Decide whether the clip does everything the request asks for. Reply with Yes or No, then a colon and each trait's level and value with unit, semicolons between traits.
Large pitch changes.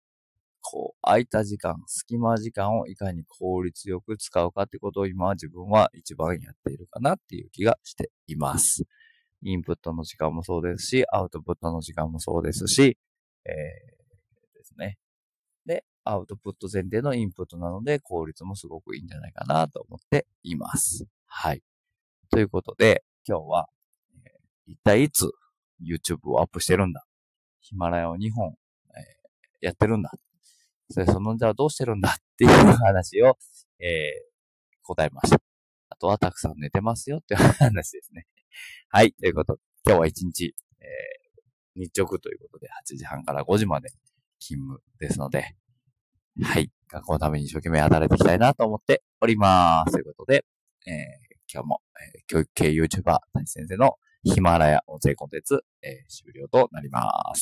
Yes: wide, 8.0 semitones